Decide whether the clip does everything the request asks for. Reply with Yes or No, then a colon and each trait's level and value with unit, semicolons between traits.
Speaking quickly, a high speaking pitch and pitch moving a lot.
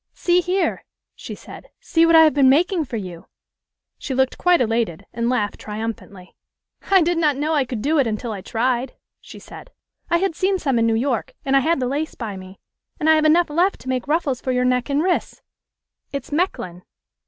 Yes: fast, 210 wpm; very high, 270 Hz; wide, 6.1 semitones